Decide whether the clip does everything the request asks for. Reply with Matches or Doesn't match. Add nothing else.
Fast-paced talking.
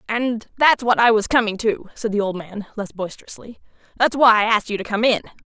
Matches